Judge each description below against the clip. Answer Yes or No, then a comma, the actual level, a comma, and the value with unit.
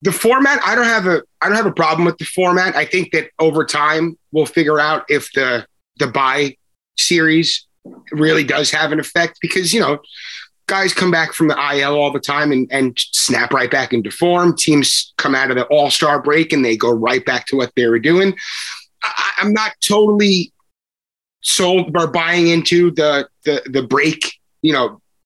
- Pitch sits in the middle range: Yes, medium, 155 Hz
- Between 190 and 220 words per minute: Yes, average, 195 wpm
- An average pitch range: Yes, average, 3.5 semitones